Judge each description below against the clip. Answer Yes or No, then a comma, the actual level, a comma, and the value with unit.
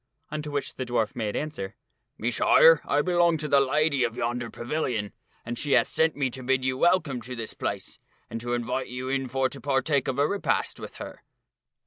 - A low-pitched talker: Yes, low, 130 Hz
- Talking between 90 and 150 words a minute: No, fast, 205 wpm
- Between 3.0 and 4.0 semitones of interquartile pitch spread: Yes, average, 3.5 semitones